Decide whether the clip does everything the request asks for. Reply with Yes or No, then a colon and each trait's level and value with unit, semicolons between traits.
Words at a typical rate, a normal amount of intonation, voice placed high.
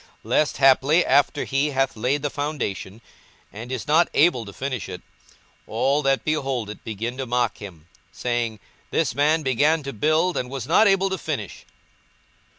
No: average, 175 wpm; average, 4.2 semitones; low, 135 Hz